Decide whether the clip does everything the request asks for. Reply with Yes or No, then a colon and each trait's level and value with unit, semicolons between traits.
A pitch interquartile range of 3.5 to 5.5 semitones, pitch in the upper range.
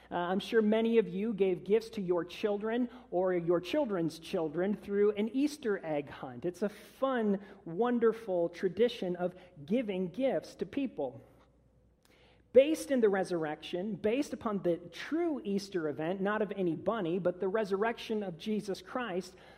Yes: average, 4.1 semitones; high, 200 Hz